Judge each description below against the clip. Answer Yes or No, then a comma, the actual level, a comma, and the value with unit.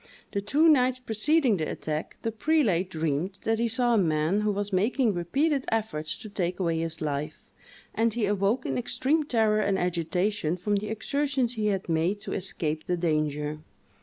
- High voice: Yes, high, 205 Hz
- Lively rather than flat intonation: Yes, wide, 5.7 semitones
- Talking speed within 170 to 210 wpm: Yes, average, 180 wpm